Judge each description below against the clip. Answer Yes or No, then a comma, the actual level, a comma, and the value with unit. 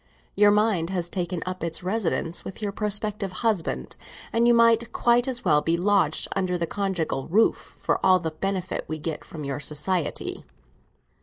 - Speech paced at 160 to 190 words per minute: Yes, average, 170 wpm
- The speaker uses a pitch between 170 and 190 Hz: Yes, medium, 185 Hz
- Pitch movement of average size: Yes, average, 4.2 semitones